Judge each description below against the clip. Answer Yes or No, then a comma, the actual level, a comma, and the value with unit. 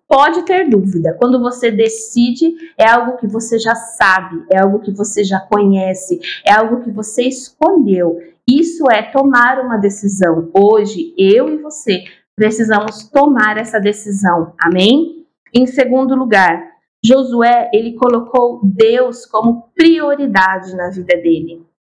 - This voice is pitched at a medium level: No, high, 225 Hz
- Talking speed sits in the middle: Yes, average, 135 wpm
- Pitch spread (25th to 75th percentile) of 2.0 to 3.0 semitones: No, average, 4.7 semitones